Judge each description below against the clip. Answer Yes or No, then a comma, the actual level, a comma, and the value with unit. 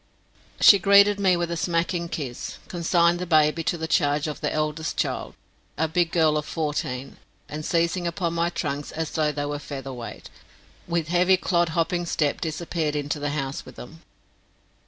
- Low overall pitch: No, medium, 160 Hz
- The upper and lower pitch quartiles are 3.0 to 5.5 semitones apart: No, narrow, 2.6 semitones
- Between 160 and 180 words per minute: Yes, average, 175 wpm